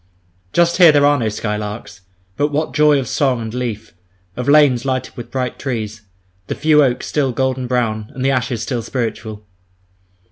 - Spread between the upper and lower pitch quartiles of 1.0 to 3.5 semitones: No, average, 4.1 semitones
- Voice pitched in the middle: No, low, 125 Hz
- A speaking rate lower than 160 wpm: No, average, 175 wpm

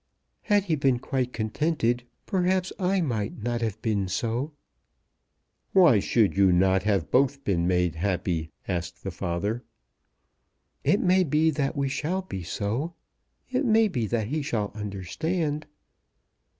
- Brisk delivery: No, average, 140 wpm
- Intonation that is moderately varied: No, wide, 8.2 semitones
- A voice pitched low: Yes, low, 120 Hz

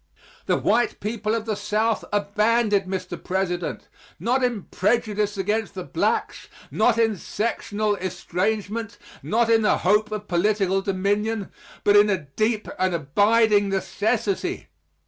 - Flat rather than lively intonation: Yes, narrow, 2.3 semitones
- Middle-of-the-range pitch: No, high, 210 Hz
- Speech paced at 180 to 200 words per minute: No, slow, 135 wpm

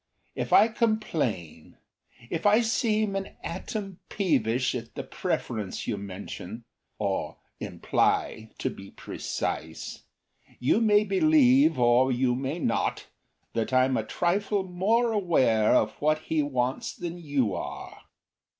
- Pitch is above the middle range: No, medium, 150 Hz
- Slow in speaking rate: Yes, slow, 125 wpm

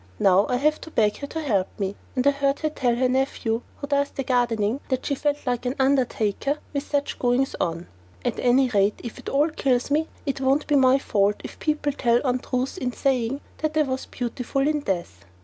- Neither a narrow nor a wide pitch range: Yes, average, 3.1 semitones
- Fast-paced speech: Yes, fast, 215 wpm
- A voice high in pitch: Yes, very high, 260 Hz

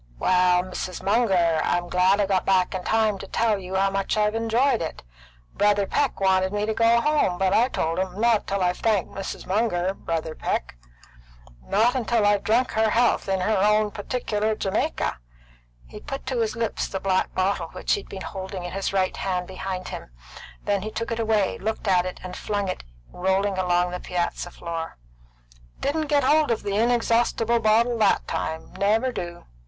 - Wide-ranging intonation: No, average, 3.3 semitones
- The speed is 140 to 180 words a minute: No, average, 190 wpm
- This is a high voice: Yes, high, 200 Hz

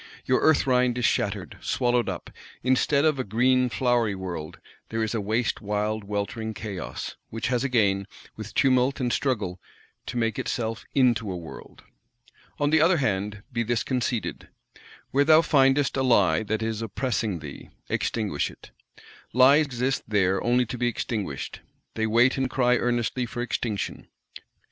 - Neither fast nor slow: Yes, average, 155 wpm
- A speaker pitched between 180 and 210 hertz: No, low, 120 Hz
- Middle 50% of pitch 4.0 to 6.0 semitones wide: No, average, 3.4 semitones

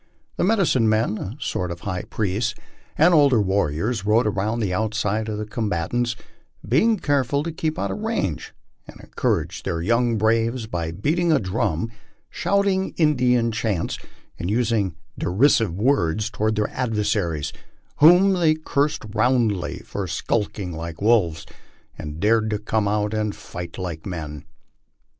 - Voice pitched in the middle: No, low, 110 Hz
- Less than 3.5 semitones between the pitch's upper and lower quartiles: No, average, 5.0 semitones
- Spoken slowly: No, average, 150 wpm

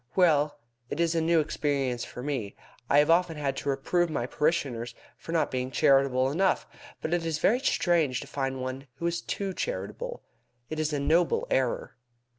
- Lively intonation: No, average, 4.2 semitones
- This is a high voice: No, medium, 150 Hz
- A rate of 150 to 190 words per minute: Yes, average, 185 wpm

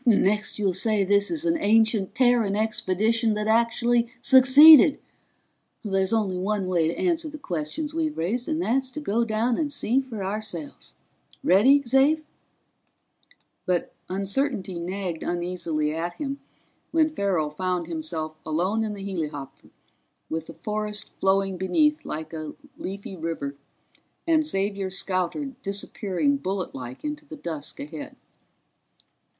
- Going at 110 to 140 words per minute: Yes, slow, 135 wpm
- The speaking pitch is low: No, high, 200 Hz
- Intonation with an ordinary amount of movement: No, wide, 6.1 semitones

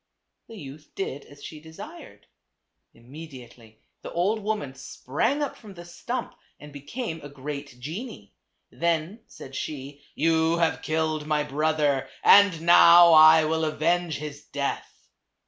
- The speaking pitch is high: No, medium, 155 Hz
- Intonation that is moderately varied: Yes, average, 3.1 semitones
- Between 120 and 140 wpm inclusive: Yes, slow, 135 wpm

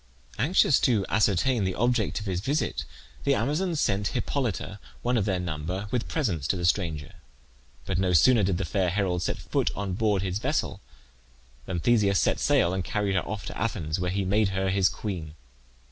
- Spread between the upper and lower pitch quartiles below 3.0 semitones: No, average, 3.7 semitones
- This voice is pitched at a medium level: No, very low, 95 Hz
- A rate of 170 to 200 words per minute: Yes, average, 190 wpm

